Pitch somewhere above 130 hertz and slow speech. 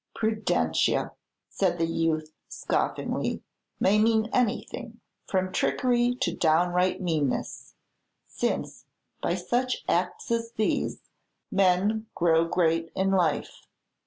Yes: medium, 185 Hz; slow, 100 wpm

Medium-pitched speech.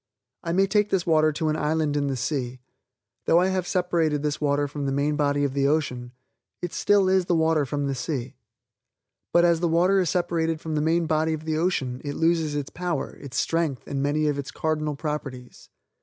Yes: medium, 155 Hz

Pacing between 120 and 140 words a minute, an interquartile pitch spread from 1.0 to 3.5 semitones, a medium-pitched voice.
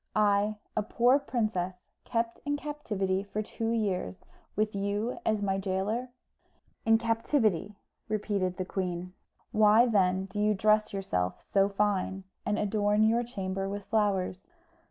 No: slow, 135 wpm; narrow, 2.4 semitones; high, 205 Hz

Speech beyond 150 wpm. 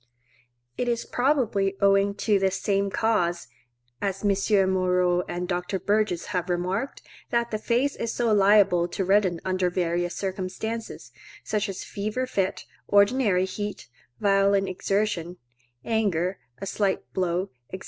No: average, 140 wpm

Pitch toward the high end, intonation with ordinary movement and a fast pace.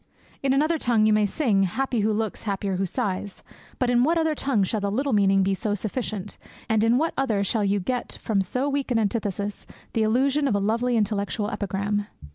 Yes: high, 215 Hz; average, 3.8 semitones; fast, 210 wpm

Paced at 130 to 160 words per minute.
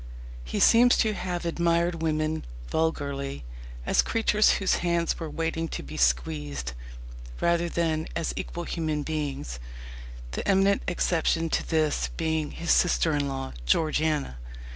Yes: slow, 135 wpm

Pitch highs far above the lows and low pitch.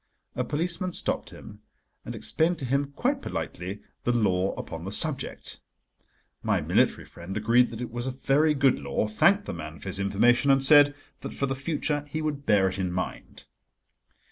Yes: wide, 6.9 semitones; low, 130 Hz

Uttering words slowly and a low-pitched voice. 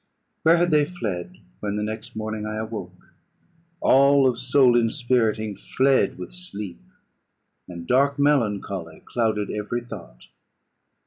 Yes: slow, 125 wpm; low, 110 Hz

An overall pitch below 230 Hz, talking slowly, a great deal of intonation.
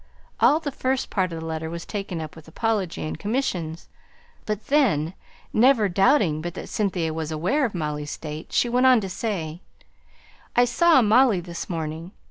No: medium, 185 Hz; average, 175 wpm; wide, 6.8 semitones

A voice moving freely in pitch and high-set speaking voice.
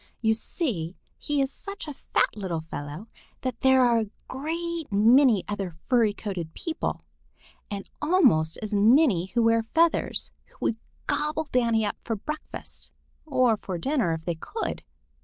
Yes: wide, 6.4 semitones; high, 230 Hz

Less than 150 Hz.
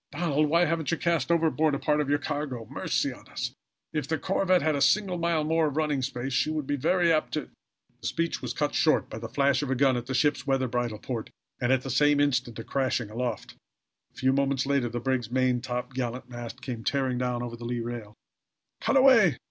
Yes: low, 135 Hz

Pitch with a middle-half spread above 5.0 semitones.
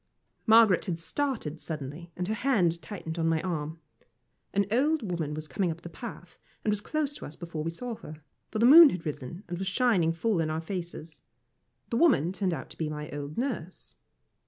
Yes: wide, 5.6 semitones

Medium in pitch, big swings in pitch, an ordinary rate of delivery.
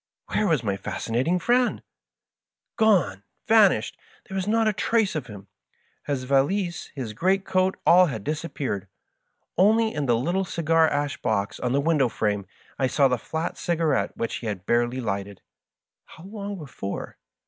Yes: medium, 150 Hz; wide, 8.1 semitones; average, 170 wpm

